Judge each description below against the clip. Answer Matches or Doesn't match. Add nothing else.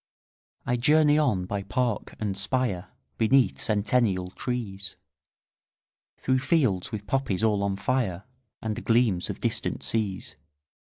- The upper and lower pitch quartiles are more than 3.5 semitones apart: Matches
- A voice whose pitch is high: Doesn't match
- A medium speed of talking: Doesn't match